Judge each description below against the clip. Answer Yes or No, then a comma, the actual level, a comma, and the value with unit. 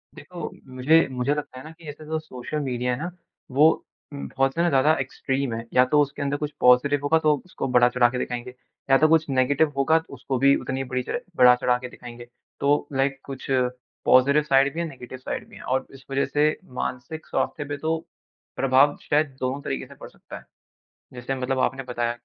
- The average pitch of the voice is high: No, low, 135 Hz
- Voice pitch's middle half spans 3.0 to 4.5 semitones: No, narrow, 2.6 semitones